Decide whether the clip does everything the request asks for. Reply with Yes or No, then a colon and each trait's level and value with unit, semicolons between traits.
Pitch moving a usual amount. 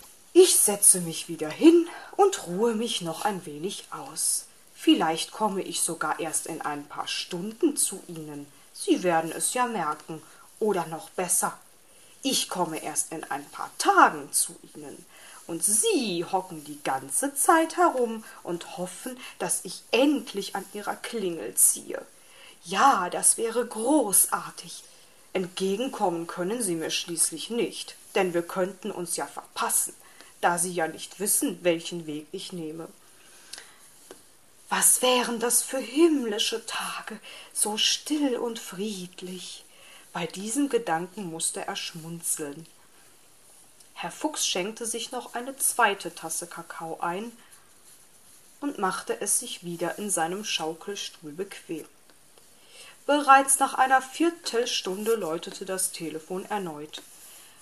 No: wide, 6.2 semitones